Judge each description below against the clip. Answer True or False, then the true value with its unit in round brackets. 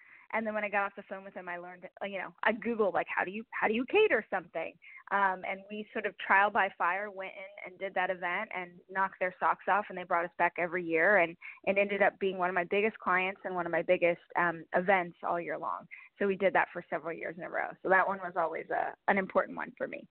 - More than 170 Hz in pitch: True (190 Hz)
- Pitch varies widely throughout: False (2.4 semitones)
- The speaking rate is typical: False (275 wpm)